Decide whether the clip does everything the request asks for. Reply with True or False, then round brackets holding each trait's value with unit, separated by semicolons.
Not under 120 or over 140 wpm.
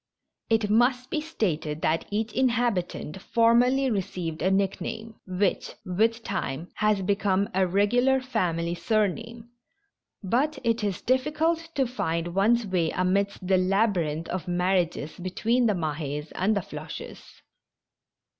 True (135 wpm)